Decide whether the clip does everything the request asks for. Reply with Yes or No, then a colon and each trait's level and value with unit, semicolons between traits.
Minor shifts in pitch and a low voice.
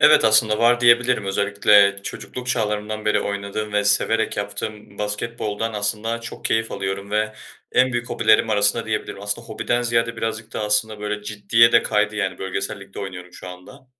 Yes: narrow, 1.9 semitones; low, 105 Hz